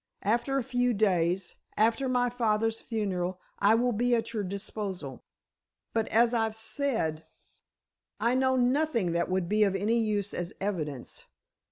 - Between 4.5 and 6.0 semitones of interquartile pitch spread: No, average, 4.1 semitones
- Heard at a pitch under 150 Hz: No, high, 220 Hz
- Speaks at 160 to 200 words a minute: No, average, 145 wpm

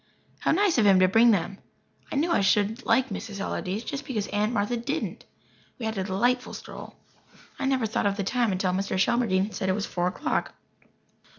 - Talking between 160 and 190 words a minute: No, average, 200 wpm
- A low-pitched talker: No, high, 215 Hz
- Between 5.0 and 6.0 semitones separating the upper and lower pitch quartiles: No, average, 4.0 semitones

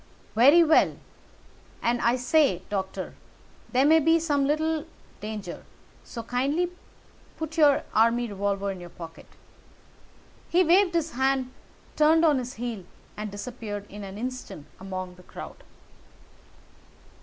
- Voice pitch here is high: Yes, very high, 250 Hz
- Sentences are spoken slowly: Yes, slow, 130 wpm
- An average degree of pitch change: No, wide, 7.2 semitones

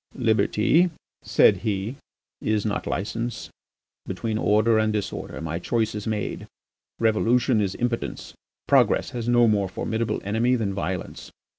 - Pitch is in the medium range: No, low, 110 Hz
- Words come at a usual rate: No, slow, 130 wpm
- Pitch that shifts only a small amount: Yes, narrow, 2.3 semitones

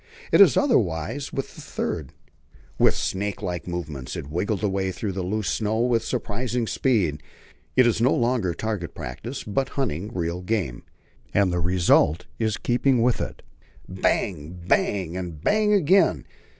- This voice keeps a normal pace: Yes, average, 150 wpm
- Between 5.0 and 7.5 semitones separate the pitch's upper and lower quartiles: Yes, wide, 5.4 semitones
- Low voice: Yes, low, 100 Hz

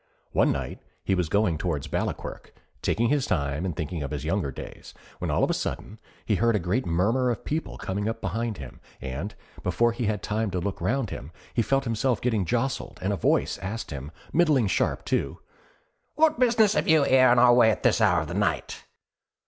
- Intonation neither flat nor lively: No, wide, 5.7 semitones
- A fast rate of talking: Yes, fast, 210 wpm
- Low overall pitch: Yes, low, 105 Hz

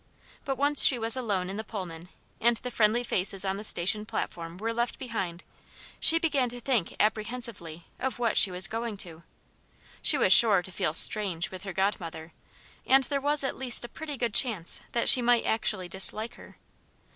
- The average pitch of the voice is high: Yes, high, 215 Hz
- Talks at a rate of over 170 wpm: Yes, average, 190 wpm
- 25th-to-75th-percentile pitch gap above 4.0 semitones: Yes, average, 4.7 semitones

